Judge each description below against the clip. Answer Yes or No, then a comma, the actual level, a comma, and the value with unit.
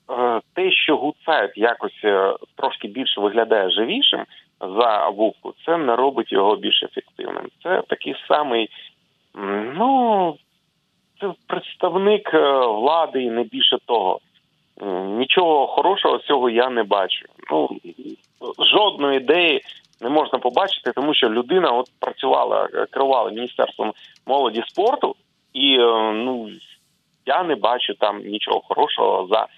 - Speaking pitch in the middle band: Yes, medium, 155 Hz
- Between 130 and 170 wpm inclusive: No, average, 115 wpm